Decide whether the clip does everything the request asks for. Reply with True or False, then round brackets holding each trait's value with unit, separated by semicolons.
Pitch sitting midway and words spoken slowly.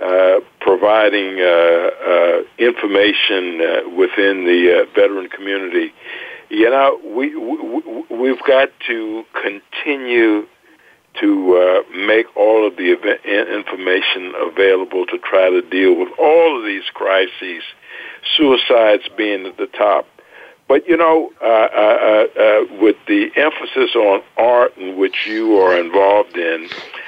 False (305 Hz; 130 wpm)